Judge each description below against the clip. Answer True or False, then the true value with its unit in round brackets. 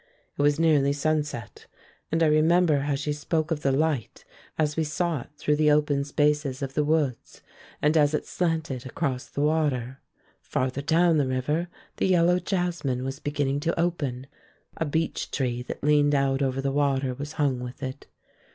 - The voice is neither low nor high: True (145 Hz)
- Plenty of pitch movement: False (2.8 semitones)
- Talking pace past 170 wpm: True (180 wpm)